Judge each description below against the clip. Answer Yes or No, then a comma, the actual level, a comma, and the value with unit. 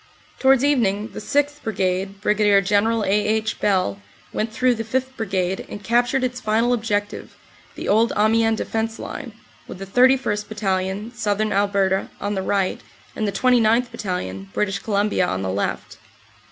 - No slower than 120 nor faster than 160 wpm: Yes, average, 155 wpm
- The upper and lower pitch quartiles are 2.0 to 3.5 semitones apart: Yes, average, 2.9 semitones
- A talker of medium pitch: No, high, 210 Hz